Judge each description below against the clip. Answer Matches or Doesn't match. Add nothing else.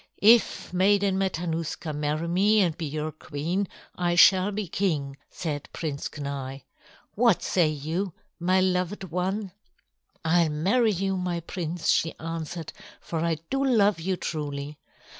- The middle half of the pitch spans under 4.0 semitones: Matches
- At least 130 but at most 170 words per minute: Matches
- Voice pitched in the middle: Matches